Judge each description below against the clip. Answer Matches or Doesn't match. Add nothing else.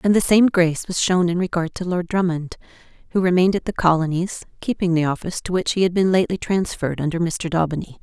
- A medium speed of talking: Doesn't match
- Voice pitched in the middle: Matches